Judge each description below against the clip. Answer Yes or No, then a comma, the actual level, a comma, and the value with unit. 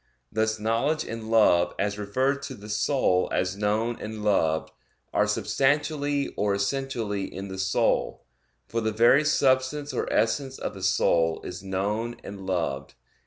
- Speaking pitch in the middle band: No, low, 110 Hz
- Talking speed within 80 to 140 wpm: No, average, 150 wpm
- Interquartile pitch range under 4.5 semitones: No, average, 5.2 semitones